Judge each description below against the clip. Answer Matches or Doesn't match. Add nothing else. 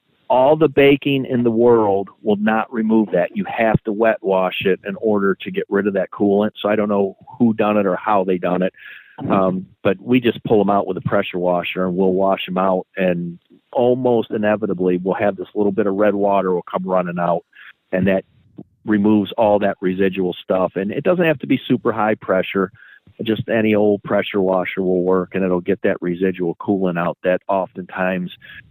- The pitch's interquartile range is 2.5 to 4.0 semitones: Matches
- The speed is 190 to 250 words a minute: Matches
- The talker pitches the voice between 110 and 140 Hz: Doesn't match